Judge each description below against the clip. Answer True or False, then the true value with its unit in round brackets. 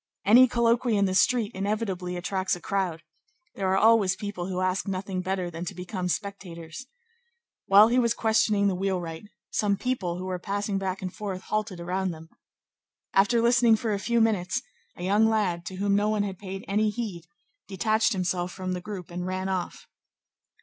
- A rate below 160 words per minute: False (185 wpm)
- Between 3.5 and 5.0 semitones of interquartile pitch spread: False (2.8 semitones)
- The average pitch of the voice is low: False (195 Hz)